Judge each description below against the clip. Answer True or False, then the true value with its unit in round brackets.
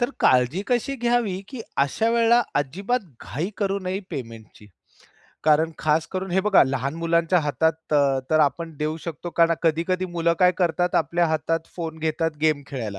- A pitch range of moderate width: True (3.7 semitones)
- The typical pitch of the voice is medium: True (165 Hz)